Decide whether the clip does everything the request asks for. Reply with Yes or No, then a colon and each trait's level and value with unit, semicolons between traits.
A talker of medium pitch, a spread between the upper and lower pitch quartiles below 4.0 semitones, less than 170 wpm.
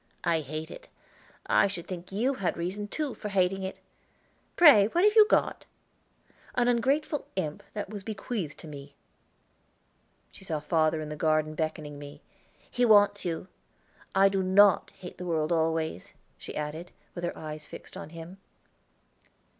No: medium, 180 Hz; average, 4.7 semitones; average, 160 wpm